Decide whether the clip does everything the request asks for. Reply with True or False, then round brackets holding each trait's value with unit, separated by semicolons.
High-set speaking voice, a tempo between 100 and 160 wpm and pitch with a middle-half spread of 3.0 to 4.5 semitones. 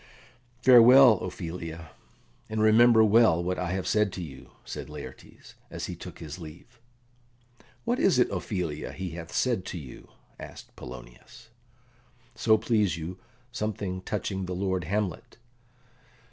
False (95 Hz; 135 wpm; 4.1 semitones)